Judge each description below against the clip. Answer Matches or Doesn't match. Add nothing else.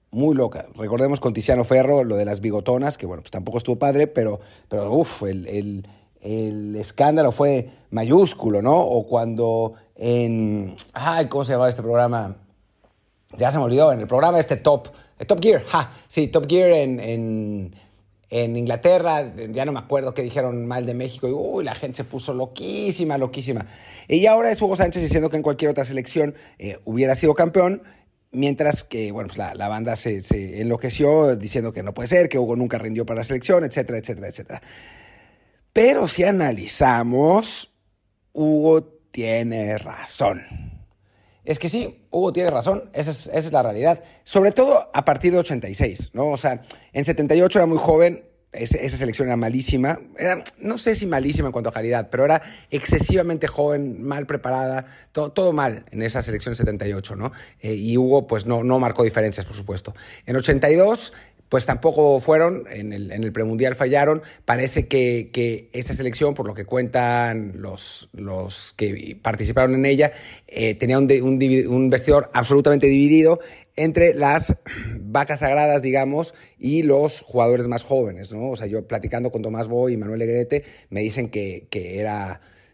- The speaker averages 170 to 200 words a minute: Matches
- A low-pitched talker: Matches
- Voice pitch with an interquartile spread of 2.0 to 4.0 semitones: Doesn't match